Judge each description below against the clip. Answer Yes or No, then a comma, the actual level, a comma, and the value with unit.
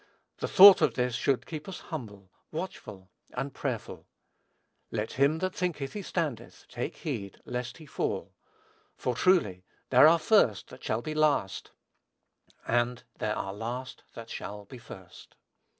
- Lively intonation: Yes, wide, 6.5 semitones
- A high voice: No, low, 125 Hz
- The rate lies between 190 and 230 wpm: No, average, 150 wpm